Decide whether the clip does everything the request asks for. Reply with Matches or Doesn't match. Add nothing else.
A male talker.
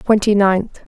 Doesn't match